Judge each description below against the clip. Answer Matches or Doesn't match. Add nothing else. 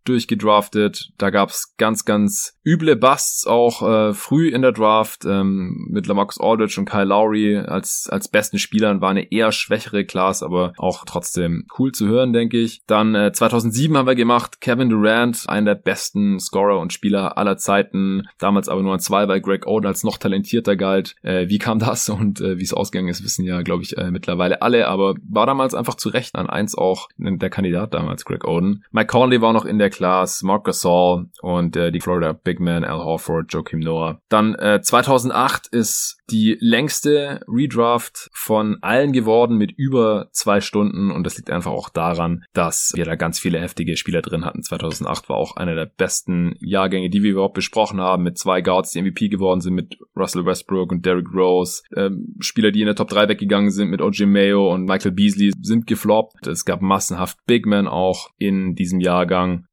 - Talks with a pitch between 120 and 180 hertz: Doesn't match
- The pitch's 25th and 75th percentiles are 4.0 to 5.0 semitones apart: Doesn't match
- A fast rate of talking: Matches